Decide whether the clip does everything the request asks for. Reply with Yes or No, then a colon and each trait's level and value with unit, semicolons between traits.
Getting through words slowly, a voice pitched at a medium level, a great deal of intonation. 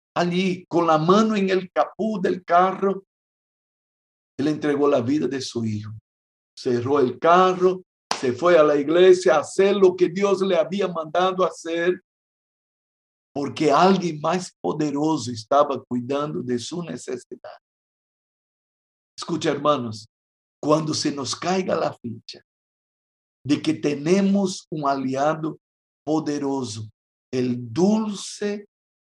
Yes: slow, 120 wpm; medium, 160 Hz; wide, 5.8 semitones